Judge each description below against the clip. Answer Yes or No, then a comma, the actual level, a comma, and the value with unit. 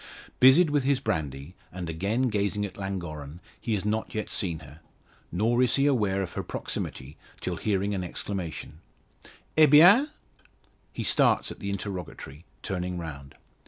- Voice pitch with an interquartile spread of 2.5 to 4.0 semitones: No, wide, 5.5 semitones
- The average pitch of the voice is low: Yes, low, 100 Hz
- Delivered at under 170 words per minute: Yes, average, 155 wpm